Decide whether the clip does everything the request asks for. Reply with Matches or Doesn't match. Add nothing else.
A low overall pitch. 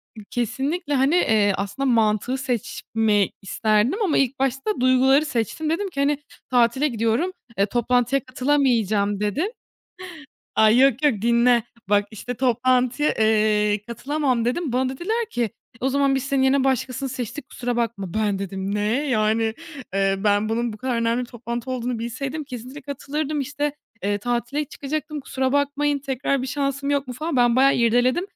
Doesn't match